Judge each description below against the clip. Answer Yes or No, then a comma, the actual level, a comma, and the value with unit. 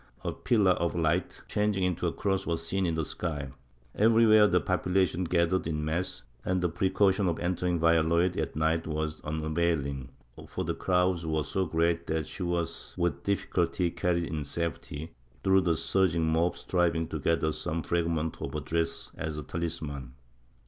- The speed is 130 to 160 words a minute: No, average, 170 wpm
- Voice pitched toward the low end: Yes, very low, 85 Hz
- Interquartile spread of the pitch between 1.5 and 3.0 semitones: Yes, narrow, 2.5 semitones